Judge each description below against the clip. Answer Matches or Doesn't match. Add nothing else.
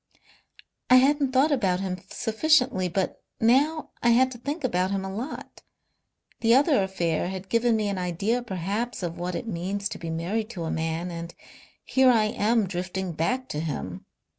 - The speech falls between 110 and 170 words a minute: Doesn't match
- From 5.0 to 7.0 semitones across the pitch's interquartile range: Matches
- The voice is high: Matches